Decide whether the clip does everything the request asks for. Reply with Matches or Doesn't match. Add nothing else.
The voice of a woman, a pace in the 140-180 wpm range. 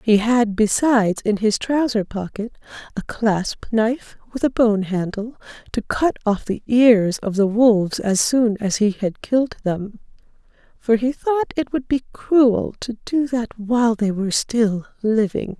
Matches